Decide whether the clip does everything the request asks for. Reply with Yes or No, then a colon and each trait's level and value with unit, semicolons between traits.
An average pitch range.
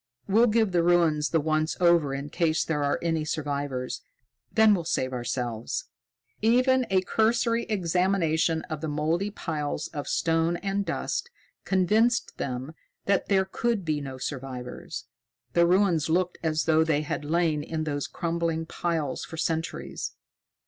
Yes: average, 4.1 semitones